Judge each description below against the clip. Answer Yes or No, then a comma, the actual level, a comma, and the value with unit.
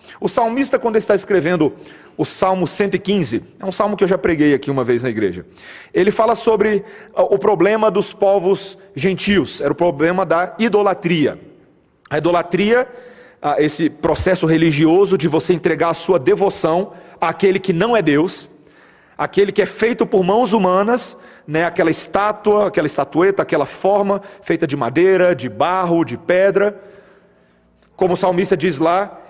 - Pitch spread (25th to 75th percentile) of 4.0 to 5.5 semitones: No, average, 3.3 semitones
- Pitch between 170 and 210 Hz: Yes, high, 190 Hz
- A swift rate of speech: No, average, 155 wpm